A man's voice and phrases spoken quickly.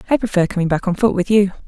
No: female; fast, 285 wpm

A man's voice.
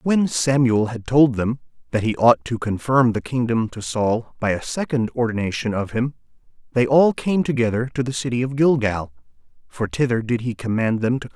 Yes: male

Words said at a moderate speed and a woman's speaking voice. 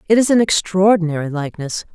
Yes: average, 155 wpm; female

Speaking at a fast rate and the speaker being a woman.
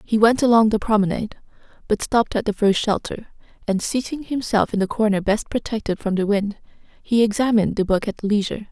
No: average, 195 wpm; female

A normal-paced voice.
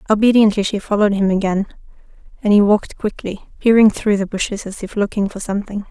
Yes: average, 185 wpm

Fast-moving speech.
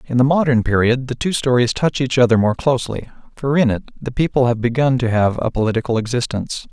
Yes: fast, 215 wpm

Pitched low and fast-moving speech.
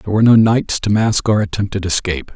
Yes: low, 105 Hz; fast, 230 wpm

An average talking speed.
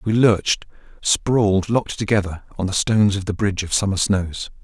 Yes: average, 180 wpm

